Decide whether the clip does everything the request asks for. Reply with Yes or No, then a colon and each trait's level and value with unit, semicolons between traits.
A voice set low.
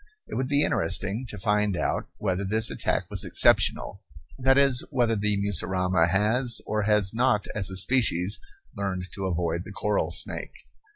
Yes: low, 105 Hz